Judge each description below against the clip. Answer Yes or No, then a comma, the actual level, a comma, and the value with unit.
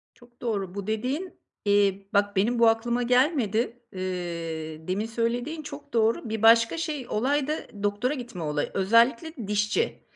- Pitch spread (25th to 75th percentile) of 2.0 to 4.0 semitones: Yes, average, 3.7 semitones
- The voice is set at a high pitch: Yes, high, 225 Hz